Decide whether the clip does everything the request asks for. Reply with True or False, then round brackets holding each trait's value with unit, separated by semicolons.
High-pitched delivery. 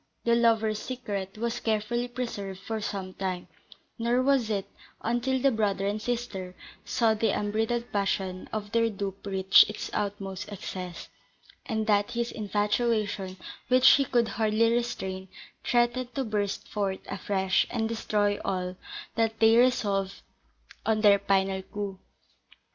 True (215 Hz)